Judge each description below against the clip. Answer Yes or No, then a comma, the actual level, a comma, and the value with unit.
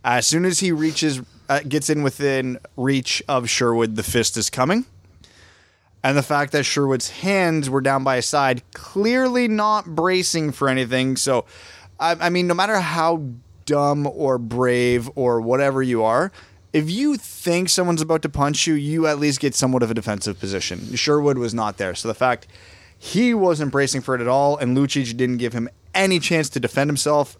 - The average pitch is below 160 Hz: Yes, low, 135 Hz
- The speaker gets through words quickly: No, average, 190 wpm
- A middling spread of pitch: Yes, average, 4.6 semitones